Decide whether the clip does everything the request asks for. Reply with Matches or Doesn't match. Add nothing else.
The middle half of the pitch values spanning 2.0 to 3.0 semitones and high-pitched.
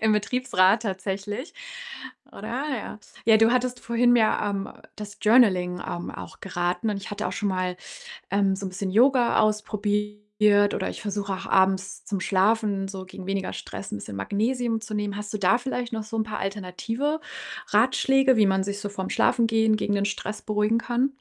Matches